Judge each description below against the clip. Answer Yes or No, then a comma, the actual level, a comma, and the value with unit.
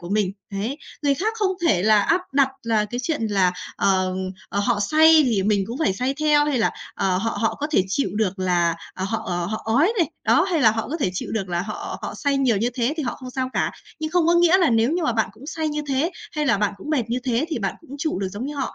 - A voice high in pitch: Yes, high, 235 Hz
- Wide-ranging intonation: Yes, wide, 6.8 semitones